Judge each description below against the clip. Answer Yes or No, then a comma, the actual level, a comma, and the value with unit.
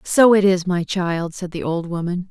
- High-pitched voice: No, medium, 180 Hz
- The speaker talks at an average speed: No, fast, 235 wpm